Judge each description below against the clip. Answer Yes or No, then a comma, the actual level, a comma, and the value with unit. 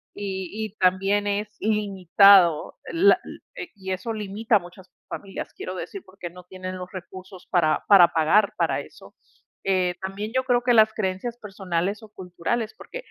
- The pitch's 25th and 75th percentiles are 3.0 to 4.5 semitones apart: No, narrow, 2.6 semitones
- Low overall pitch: No, high, 195 Hz